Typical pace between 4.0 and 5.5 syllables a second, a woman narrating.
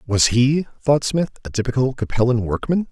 No: 5.0 syllables/s; male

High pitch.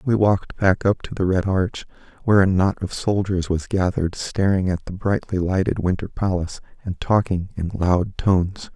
No: very low, 95 Hz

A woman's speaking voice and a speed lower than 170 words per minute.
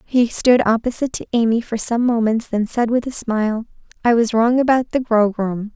No: female; average, 200 wpm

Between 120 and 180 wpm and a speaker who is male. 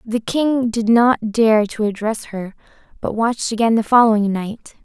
No: average, 175 wpm; female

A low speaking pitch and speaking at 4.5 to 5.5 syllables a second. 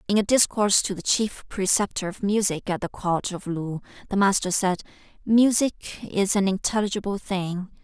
No: high, 195 Hz; 5.1 syllables/s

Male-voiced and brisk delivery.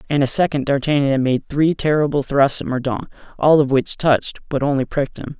Yes: male; fast, 210 wpm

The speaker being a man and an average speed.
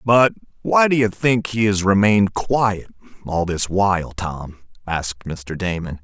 Yes: male; average, 160 wpm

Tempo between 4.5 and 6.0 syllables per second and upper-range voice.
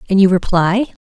Yes: 5.6 syllables/s; high, 195 Hz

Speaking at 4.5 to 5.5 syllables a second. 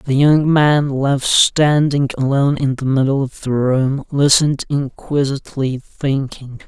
No: 4.3 syllables/s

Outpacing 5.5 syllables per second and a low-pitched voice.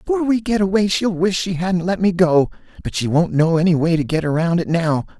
No: 5.8 syllables/s; medium, 175 Hz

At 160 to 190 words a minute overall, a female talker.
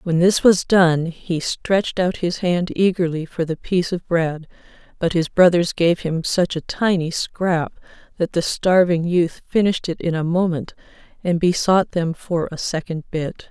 Yes: average, 180 wpm; female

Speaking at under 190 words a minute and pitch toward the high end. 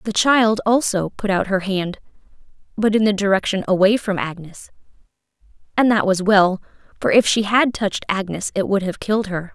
Yes: average, 175 wpm; high, 200 Hz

